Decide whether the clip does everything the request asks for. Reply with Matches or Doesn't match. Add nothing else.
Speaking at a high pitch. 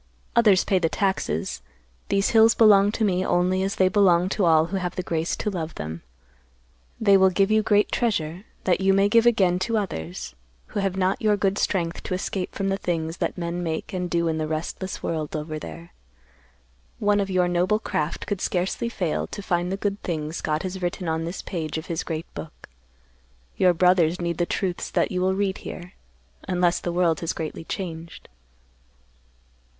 Doesn't match